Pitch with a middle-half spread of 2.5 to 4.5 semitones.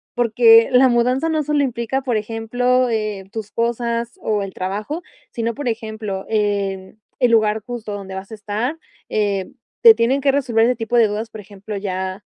Yes: average, 2.9 semitones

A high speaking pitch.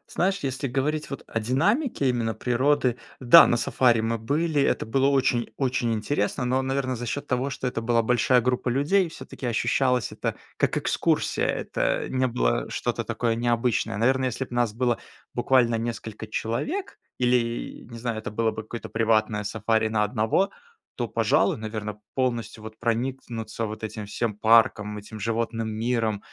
No: low, 120 Hz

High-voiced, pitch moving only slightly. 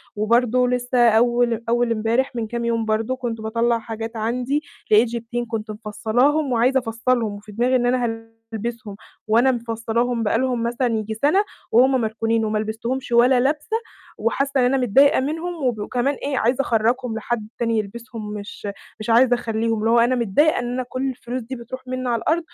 Yes: high, 235 Hz; narrow, 2.2 semitones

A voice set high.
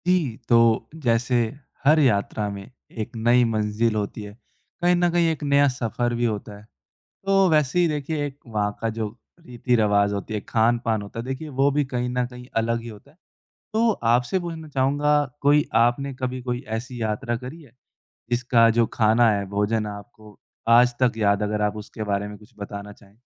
No: low, 120 Hz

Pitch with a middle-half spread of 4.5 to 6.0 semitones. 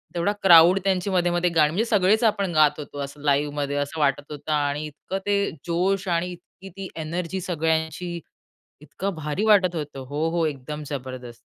No: average, 4.0 semitones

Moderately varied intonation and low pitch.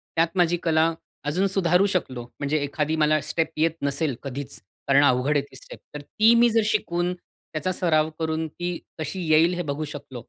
No: average, 3.5 semitones; medium, 160 Hz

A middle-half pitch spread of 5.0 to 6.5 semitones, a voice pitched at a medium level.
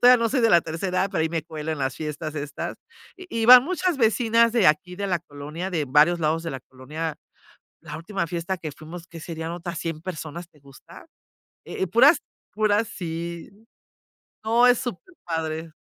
Yes: average, 5.3 semitones; medium, 170 Hz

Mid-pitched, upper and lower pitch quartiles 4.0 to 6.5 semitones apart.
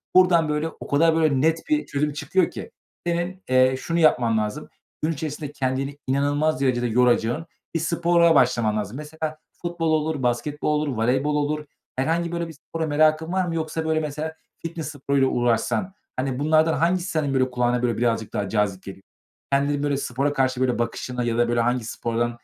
Yes: medium, 145 Hz; average, 4.4 semitones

